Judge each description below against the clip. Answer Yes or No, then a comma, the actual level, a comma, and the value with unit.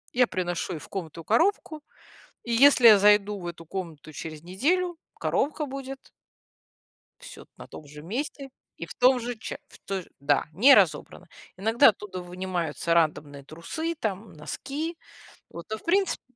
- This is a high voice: Yes, high, 205 Hz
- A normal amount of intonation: No, wide, 8.3 semitones